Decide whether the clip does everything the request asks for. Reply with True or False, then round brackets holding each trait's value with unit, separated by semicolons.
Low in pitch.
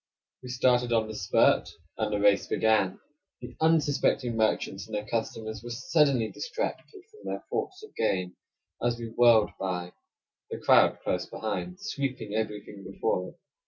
True (110 Hz)